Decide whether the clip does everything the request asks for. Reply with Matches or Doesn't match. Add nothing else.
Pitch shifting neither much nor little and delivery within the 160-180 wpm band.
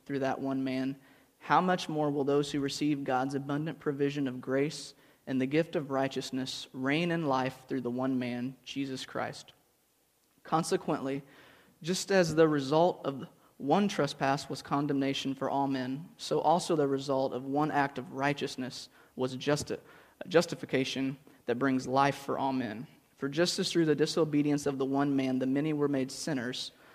Doesn't match